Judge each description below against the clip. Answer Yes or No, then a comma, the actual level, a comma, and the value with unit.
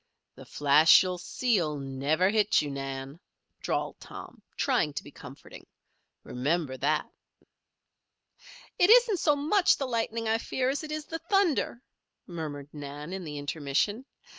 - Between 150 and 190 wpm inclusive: No, average, 140 wpm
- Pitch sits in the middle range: Yes, medium, 180 Hz